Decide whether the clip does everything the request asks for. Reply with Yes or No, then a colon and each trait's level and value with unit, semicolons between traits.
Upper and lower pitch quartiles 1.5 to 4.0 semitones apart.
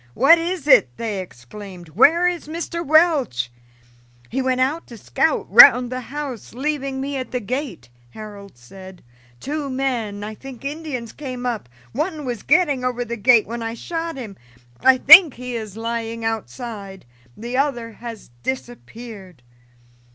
No: average, 4.5 semitones